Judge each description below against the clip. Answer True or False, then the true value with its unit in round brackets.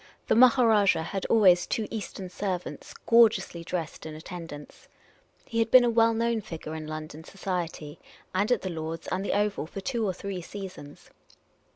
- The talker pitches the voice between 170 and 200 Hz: True (190 Hz)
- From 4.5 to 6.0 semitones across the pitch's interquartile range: True (5.2 semitones)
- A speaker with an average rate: True (170 wpm)